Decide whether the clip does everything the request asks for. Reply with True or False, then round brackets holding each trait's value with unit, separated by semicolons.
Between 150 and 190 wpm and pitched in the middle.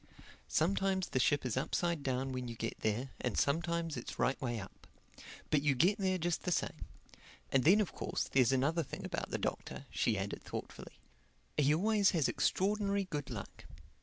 True (180 wpm; 150 Hz)